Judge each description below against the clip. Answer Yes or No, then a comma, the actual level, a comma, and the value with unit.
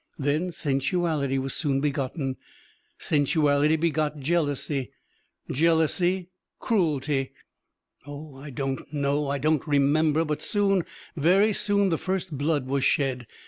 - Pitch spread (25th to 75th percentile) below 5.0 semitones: Yes, average, 3.2 semitones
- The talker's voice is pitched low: No, medium, 150 Hz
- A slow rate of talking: Yes, slow, 115 wpm